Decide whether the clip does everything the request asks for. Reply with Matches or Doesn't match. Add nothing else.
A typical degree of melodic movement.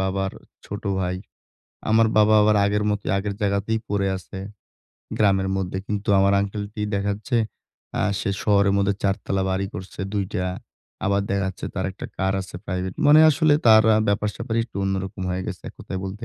Doesn't match